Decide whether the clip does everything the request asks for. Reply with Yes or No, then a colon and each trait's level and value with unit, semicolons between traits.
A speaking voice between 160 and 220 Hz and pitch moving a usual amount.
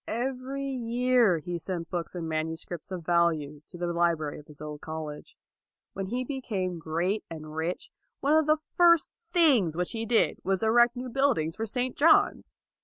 No: medium, 185 Hz; wide, 7.5 semitones